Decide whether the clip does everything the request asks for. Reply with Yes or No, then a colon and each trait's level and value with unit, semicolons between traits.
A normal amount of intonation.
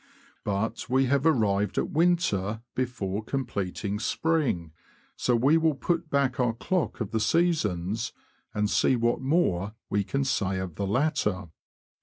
No: wide, 5.9 semitones